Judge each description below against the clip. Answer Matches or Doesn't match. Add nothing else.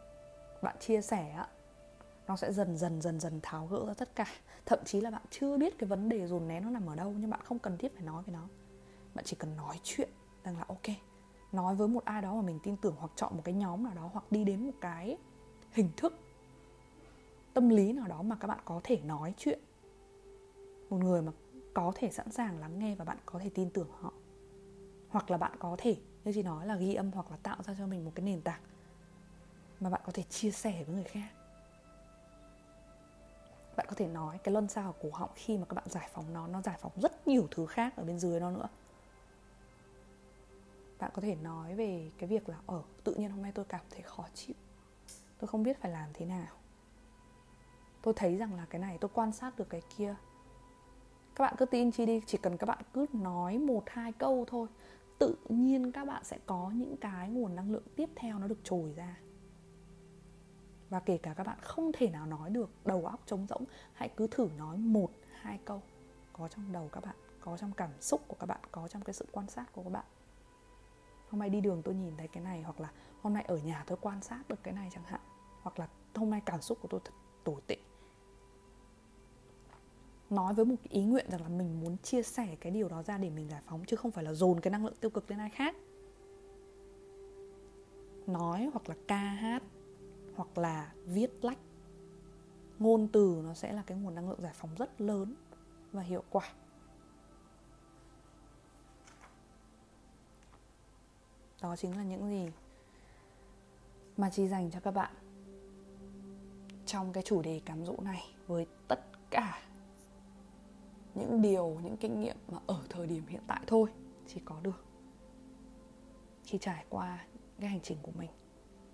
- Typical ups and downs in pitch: Matches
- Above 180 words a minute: Matches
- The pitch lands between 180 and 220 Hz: Matches